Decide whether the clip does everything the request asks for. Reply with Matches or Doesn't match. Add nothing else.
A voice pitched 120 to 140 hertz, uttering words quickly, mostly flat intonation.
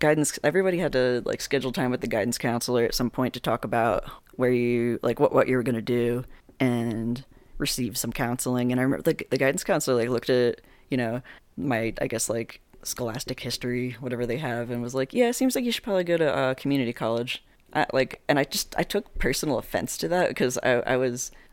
Matches